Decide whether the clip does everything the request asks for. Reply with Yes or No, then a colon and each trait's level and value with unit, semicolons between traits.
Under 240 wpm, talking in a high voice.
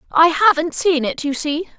Yes: average, 200 wpm; very high, 320 Hz